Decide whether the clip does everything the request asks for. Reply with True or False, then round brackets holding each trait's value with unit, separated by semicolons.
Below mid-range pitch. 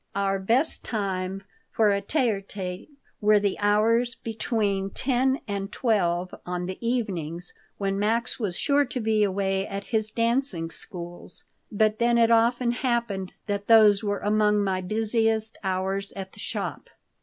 False (205 Hz)